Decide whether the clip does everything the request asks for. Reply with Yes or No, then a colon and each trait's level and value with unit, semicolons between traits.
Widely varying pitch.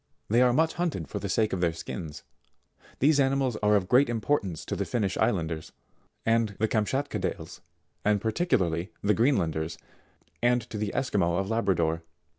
Yes: wide, 5.8 semitones